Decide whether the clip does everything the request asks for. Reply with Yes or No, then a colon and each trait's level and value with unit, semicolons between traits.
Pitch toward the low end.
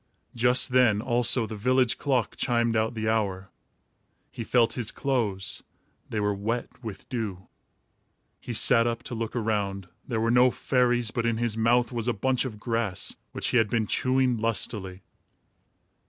Yes: low, 115 Hz